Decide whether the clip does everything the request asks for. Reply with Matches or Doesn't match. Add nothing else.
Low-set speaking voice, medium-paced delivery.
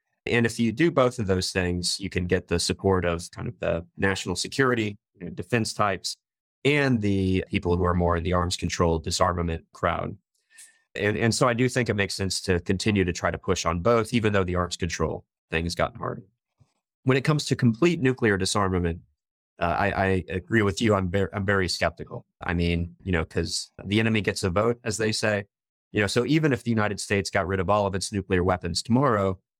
Doesn't match